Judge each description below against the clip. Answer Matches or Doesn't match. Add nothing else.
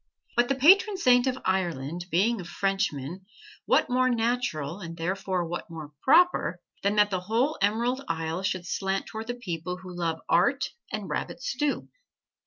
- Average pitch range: Doesn't match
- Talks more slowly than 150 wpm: Doesn't match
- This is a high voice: Matches